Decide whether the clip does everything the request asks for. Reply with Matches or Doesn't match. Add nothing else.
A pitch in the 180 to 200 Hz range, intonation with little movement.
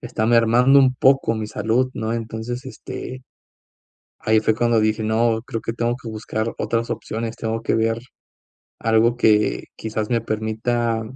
Doesn't match